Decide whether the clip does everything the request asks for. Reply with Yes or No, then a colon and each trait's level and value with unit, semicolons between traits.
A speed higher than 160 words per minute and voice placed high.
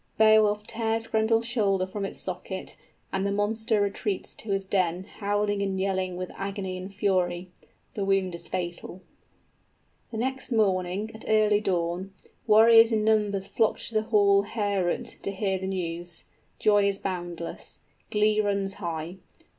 No: average, 150 wpm; high, 200 Hz